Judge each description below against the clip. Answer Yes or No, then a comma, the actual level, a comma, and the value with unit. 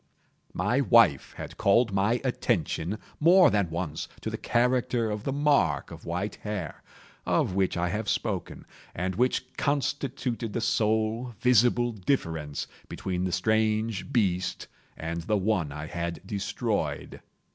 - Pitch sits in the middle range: No, low, 105 Hz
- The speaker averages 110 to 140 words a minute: Yes, slow, 135 wpm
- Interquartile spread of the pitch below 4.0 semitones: No, average, 5.1 semitones